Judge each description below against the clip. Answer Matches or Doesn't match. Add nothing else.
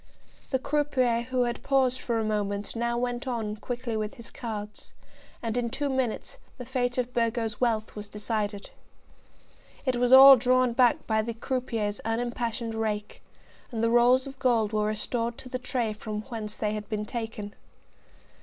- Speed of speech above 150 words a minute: Matches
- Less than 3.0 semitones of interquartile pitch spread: Matches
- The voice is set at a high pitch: Matches